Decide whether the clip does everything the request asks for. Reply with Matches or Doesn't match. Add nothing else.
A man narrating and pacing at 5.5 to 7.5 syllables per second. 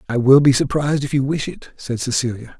Matches